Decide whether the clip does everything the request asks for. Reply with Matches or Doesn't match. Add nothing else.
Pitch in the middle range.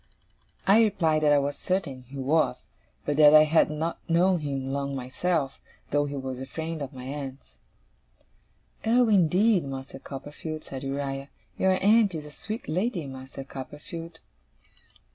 Matches